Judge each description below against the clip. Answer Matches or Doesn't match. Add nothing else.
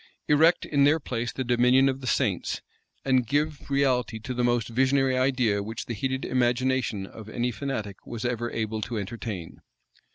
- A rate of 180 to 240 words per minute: Doesn't match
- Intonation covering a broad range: Doesn't match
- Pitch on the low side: Matches